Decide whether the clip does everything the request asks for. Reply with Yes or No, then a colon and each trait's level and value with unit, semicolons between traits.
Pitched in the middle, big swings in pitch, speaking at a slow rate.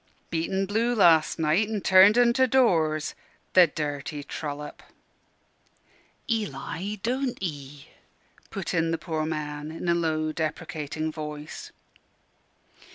No: medium, 160 Hz; average, 4.5 semitones; slow, 125 wpm